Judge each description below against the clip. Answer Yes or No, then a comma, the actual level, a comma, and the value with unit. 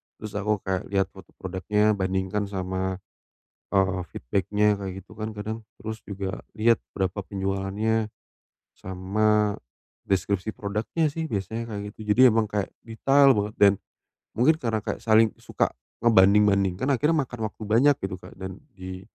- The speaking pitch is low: Yes, low, 105 Hz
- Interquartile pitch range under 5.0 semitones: Yes, narrow, 2.5 semitones